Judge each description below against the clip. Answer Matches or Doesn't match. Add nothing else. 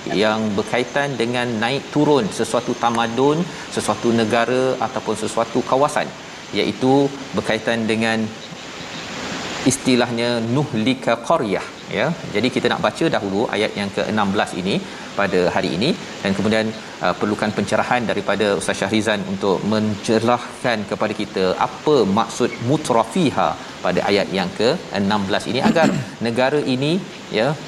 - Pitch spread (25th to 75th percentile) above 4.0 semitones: Doesn't match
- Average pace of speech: Matches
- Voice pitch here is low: Matches